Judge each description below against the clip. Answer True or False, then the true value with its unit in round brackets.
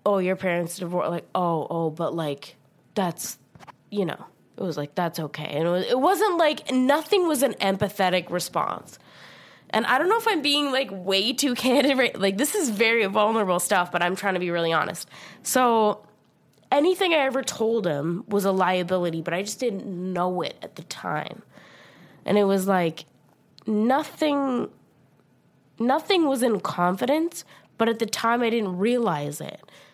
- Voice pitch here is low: False (200 Hz)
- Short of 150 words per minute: False (175 wpm)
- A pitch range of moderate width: False (6.8 semitones)